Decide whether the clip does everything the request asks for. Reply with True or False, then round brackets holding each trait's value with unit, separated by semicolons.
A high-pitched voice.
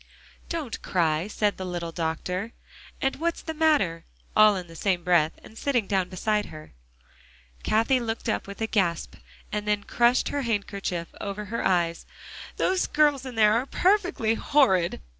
True (210 Hz)